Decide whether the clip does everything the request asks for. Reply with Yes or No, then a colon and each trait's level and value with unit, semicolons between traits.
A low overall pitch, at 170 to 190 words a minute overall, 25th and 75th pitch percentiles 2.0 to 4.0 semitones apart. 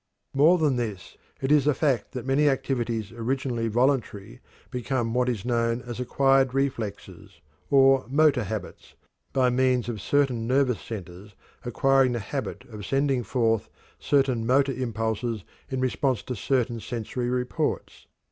No: low, 125 Hz; average, 140 wpm; average, 2.9 semitones